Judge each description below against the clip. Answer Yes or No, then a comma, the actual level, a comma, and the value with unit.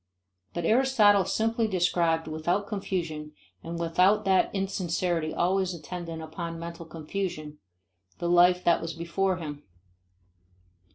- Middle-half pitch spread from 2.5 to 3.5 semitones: Yes, average, 2.8 semitones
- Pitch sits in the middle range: Yes, medium, 175 Hz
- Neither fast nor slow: No, slow, 115 wpm